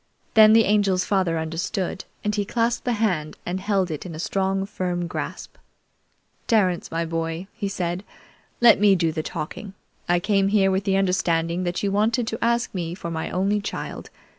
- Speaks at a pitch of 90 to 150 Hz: No, high, 190 Hz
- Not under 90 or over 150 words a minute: No, average, 185 wpm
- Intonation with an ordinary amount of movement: Yes, average, 3.2 semitones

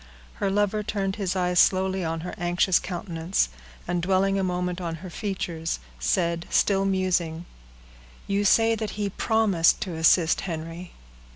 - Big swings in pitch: No, narrow, 2.5 semitones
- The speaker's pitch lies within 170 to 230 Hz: Yes, medium, 185 Hz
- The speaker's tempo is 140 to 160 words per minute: Yes, average, 150 wpm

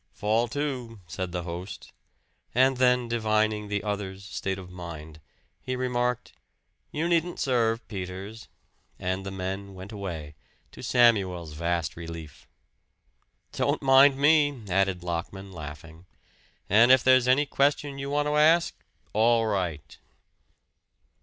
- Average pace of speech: No, slow, 125 wpm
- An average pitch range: No, wide, 5.9 semitones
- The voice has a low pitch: Yes, low, 105 Hz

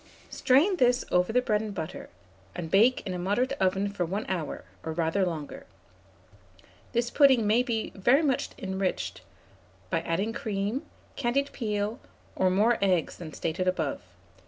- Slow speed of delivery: No, average, 155 wpm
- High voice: Yes, high, 205 Hz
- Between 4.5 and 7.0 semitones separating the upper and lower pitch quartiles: Yes, average, 5.0 semitones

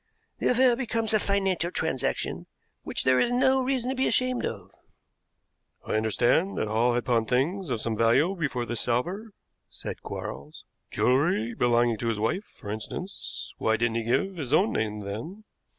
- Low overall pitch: Yes, low, 130 Hz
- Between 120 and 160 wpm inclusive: No, average, 170 wpm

